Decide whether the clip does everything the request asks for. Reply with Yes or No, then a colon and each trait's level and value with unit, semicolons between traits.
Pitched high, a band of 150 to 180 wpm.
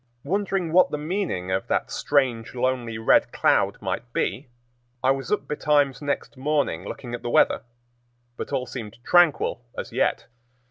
No: low, 135 Hz; average, 155 wpm